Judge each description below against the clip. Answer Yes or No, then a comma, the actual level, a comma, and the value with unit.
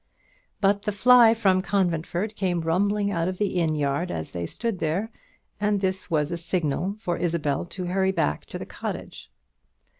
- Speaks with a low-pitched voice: No, medium, 185 Hz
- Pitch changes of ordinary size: Yes, average, 3.5 semitones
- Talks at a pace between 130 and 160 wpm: No, average, 175 wpm